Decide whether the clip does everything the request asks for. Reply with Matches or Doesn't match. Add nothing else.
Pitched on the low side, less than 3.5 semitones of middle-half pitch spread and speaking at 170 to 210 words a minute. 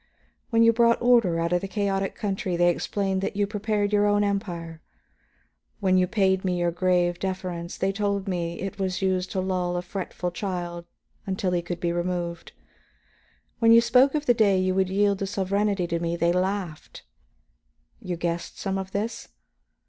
Doesn't match